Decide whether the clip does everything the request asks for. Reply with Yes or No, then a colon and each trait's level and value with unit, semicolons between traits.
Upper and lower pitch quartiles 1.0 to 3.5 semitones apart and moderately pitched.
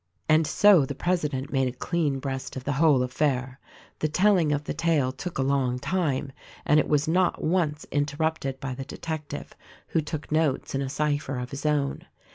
Yes: average, 2.9 semitones; medium, 145 Hz